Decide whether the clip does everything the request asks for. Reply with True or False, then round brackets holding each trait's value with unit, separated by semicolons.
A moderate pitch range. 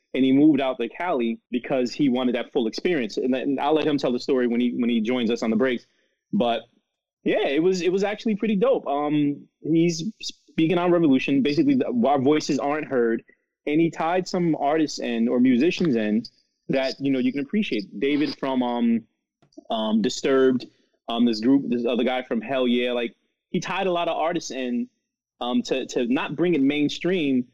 False (6.6 semitones)